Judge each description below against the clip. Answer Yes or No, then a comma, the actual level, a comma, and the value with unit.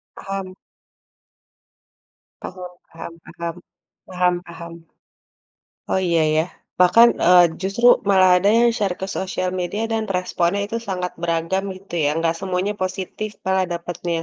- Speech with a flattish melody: Yes, narrow, 2.1 semitones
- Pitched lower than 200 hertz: Yes, medium, 185 Hz